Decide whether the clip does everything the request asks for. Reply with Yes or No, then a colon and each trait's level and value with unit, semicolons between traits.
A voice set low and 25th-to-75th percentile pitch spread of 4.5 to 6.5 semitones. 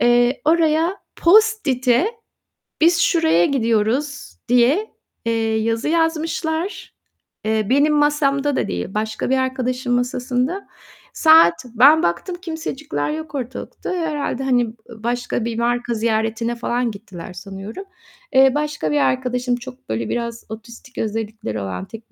No: high, 245 Hz; average, 5.1 semitones